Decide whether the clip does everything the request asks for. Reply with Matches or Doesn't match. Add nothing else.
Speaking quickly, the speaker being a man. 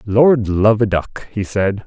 Doesn't match